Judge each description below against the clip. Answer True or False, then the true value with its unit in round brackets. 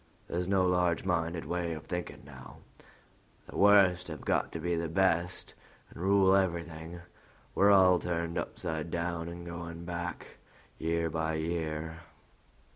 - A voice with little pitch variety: True (1.5 semitones)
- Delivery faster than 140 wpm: False (135 wpm)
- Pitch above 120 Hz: False (85 Hz)